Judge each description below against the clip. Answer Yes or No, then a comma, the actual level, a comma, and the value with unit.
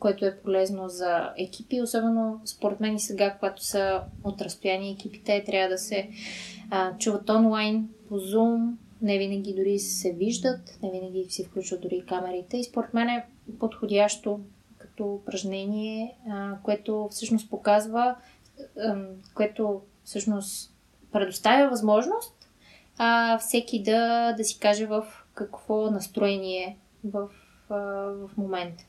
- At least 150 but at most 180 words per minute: No, average, 125 wpm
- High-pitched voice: Yes, high, 205 Hz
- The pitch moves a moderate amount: No, narrow, 2.3 semitones